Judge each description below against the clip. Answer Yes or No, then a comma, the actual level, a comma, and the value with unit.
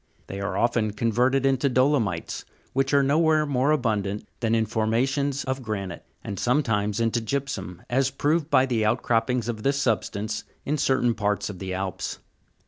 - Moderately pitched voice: No, low, 120 Hz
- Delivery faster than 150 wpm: Yes, average, 165 wpm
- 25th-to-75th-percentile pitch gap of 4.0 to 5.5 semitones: Yes, average, 4.3 semitones